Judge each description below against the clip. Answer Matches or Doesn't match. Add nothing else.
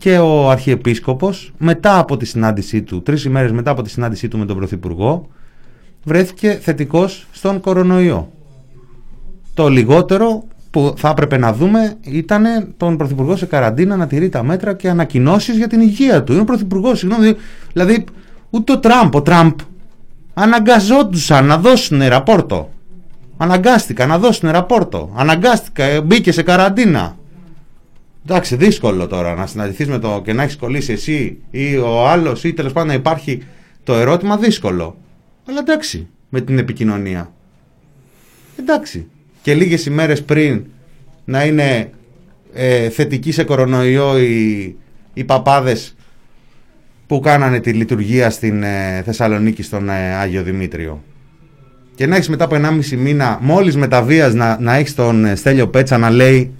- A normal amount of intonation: Doesn't match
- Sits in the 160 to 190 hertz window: Doesn't match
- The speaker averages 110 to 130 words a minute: Doesn't match